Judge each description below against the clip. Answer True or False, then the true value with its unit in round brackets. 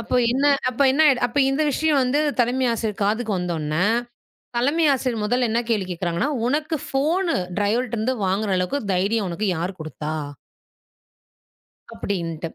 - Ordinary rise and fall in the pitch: False (6.3 semitones)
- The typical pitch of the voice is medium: False (230 Hz)